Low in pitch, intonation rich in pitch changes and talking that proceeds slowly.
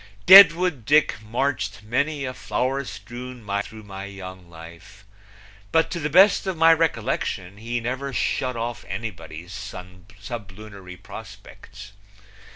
Yes: low, 115 Hz; wide, 6.1 semitones; slow, 125 wpm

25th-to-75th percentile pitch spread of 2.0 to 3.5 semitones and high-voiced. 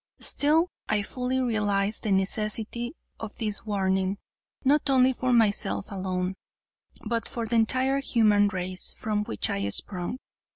No: average, 4.3 semitones; high, 215 Hz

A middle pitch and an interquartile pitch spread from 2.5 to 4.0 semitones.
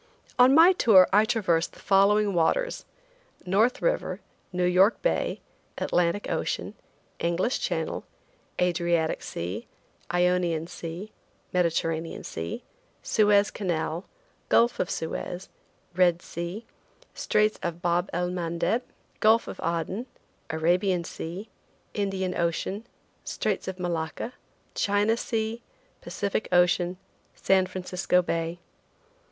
Yes: medium, 180 Hz; average, 3.4 semitones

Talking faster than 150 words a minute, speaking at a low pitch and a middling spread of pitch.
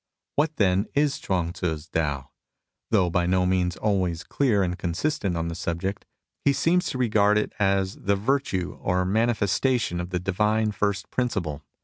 Yes: average, 185 wpm; very low, 95 Hz; average, 3.8 semitones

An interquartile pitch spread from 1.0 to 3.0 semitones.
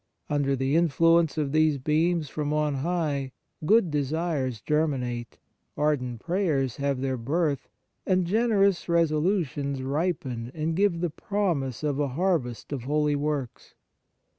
No: average, 3.8 semitones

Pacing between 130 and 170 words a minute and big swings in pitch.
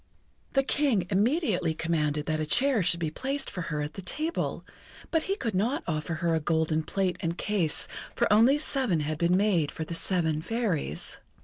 No: average, 190 wpm; wide, 6.7 semitones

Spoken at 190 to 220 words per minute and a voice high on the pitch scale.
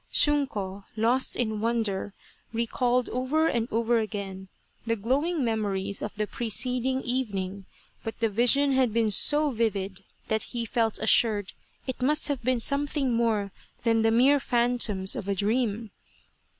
No: average, 145 wpm; high, 230 Hz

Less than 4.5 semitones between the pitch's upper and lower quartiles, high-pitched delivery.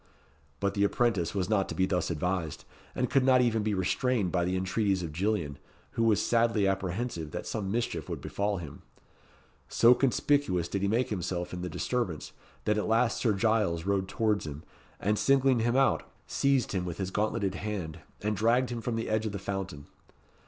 No: average, 4.0 semitones; low, 100 Hz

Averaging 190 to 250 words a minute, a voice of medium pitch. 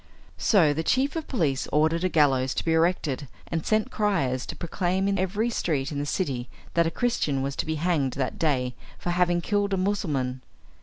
Yes: average, 200 wpm; medium, 165 Hz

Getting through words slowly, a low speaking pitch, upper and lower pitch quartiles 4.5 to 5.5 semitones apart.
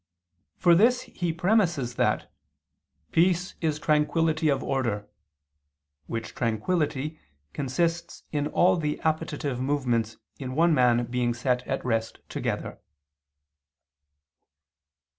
No: slow, 105 wpm; medium, 150 Hz; average, 5.2 semitones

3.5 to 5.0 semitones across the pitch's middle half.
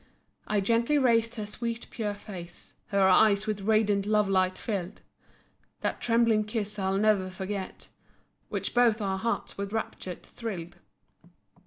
No: narrow, 2.6 semitones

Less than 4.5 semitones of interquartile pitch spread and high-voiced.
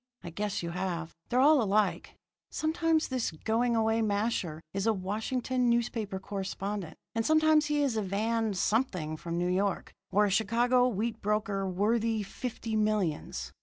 Yes: average, 3.6 semitones; high, 215 Hz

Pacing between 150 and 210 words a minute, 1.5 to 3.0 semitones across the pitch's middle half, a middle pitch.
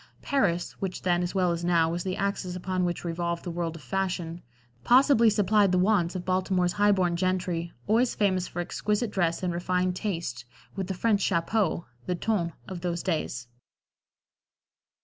Yes: average, 170 wpm; narrow, 2.4 semitones; medium, 180 Hz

